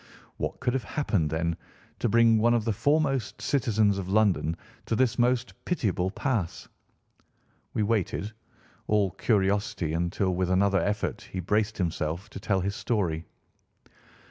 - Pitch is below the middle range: Yes, low, 105 Hz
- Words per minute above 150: No, average, 145 wpm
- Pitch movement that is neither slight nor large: Yes, average, 3.9 semitones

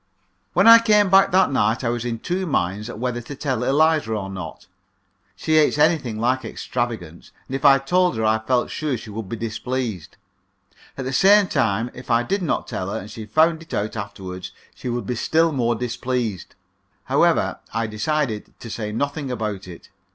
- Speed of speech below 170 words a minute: No, average, 190 wpm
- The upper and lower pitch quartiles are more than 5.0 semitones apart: Yes, wide, 5.6 semitones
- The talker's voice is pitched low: Yes, low, 120 Hz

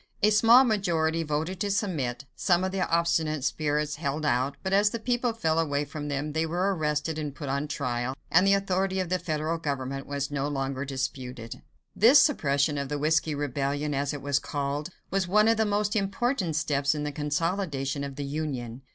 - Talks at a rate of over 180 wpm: Yes, average, 195 wpm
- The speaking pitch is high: No, medium, 150 Hz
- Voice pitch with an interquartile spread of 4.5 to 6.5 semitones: Yes, average, 4.8 semitones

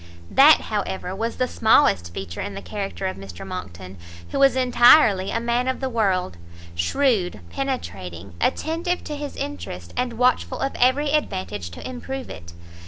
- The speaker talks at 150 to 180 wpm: Yes, average, 160 wpm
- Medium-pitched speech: No, high, 200 Hz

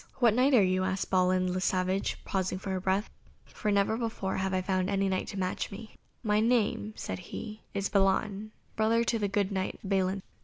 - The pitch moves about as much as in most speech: No, narrow, 2.3 semitones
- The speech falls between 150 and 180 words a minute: No, average, 195 wpm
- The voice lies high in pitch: Yes, high, 195 Hz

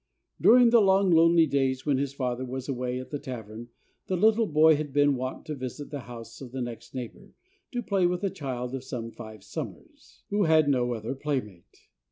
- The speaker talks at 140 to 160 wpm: No, fast, 205 wpm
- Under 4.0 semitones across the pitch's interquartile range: No, average, 4.5 semitones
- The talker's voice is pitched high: No, low, 135 Hz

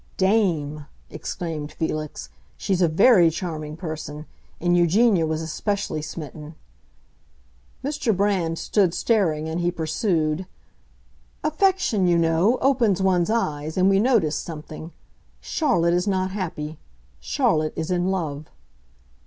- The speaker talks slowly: Yes, slow, 120 wpm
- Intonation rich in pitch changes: No, average, 3.9 semitones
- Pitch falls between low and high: Yes, medium, 170 Hz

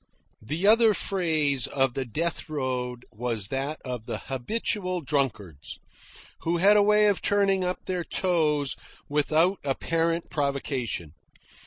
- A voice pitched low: No, medium, 150 Hz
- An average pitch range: No, wide, 5.8 semitones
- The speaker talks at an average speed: No, slow, 130 wpm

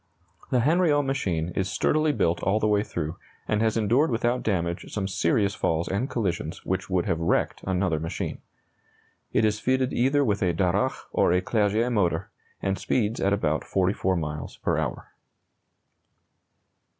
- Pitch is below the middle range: Yes, low, 100 Hz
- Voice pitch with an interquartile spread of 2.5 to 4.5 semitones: No, average, 5.1 semitones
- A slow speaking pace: No, average, 160 wpm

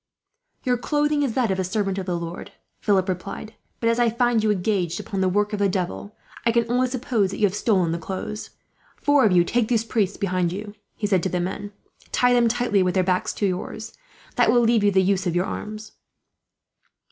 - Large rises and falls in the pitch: No, average, 3.8 semitones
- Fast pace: Yes, fast, 225 wpm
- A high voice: Yes, high, 205 Hz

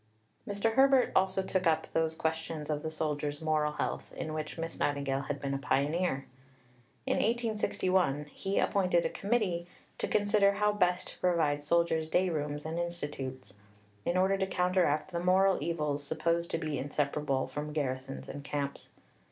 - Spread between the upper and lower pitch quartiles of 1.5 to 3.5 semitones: No, average, 3.9 semitones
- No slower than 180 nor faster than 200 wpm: No, average, 160 wpm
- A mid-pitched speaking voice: Yes, medium, 160 Hz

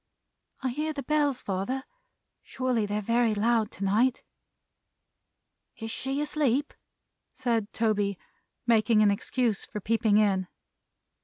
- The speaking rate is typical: No, slow, 115 wpm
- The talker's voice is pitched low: No, high, 230 Hz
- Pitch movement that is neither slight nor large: Yes, average, 3.7 semitones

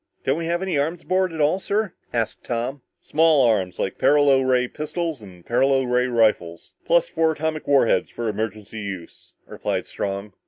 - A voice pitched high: No, low, 135 Hz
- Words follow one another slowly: No, average, 180 wpm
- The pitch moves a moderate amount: No, wide, 6.4 semitones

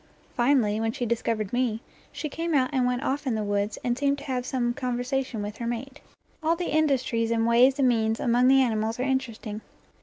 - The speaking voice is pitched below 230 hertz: No, high, 245 Hz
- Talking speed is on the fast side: Yes, fast, 210 wpm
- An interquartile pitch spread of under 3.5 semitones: Yes, average, 3.0 semitones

